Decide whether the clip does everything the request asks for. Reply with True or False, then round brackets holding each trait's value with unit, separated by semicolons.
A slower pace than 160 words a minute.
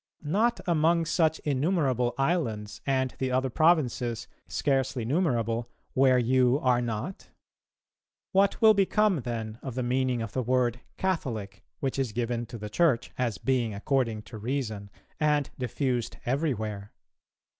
True (140 wpm)